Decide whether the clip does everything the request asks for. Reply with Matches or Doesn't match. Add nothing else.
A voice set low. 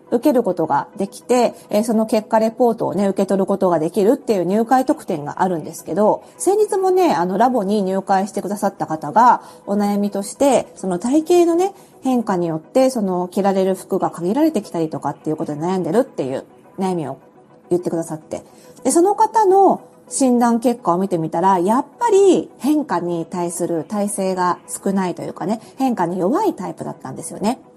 Doesn't match